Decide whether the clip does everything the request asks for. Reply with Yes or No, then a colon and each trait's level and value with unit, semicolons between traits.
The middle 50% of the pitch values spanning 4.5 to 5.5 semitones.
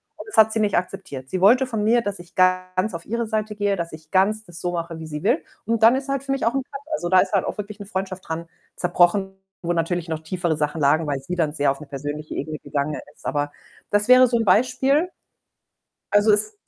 Yes: average, 5.1 semitones